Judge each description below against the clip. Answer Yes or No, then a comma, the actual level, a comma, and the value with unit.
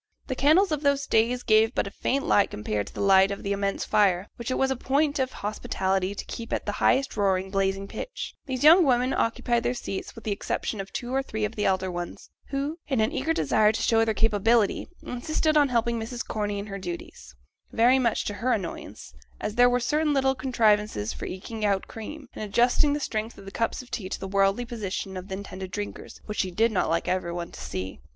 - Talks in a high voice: Yes, high, 220 Hz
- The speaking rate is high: Yes, fast, 230 wpm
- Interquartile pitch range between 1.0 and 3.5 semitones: No, average, 4.5 semitones